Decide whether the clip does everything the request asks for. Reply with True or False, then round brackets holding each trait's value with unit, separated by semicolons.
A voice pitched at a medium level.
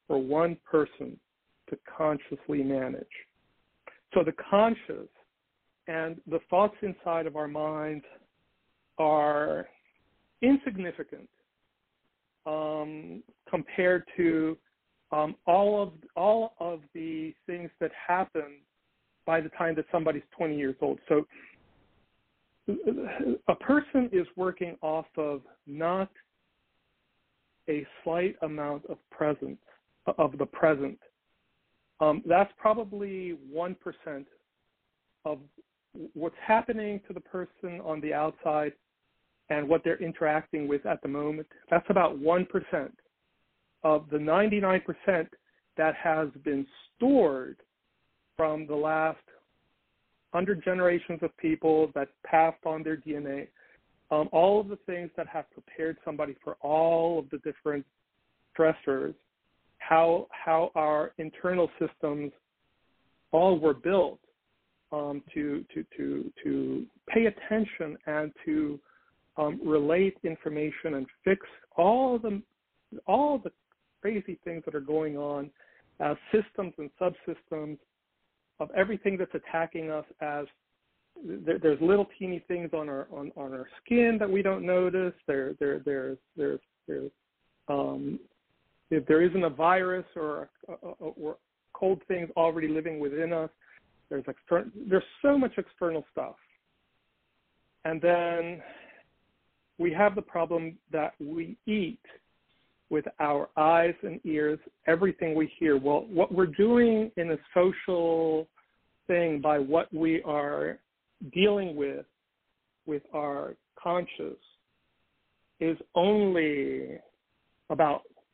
True (160 Hz)